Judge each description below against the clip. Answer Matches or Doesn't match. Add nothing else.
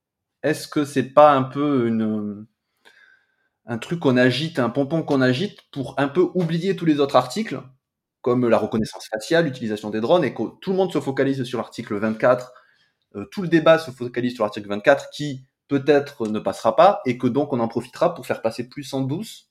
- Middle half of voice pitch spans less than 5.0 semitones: Doesn't match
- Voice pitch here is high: Doesn't match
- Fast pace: Doesn't match